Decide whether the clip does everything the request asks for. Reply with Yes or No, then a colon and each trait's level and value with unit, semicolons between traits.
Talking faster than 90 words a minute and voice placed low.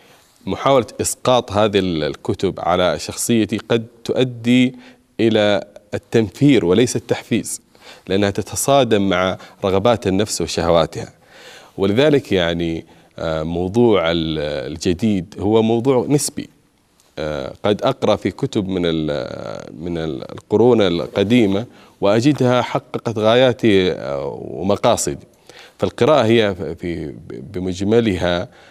No: average, 85 wpm; low, 105 Hz